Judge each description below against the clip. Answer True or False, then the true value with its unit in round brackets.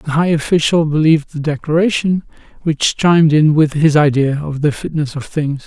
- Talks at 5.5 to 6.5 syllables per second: False (5.1 syllables/s)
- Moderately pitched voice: True (155 Hz)